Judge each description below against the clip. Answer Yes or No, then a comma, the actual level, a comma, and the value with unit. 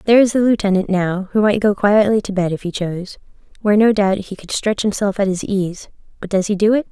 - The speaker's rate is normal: No, fast, 250 wpm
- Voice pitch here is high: Yes, high, 200 Hz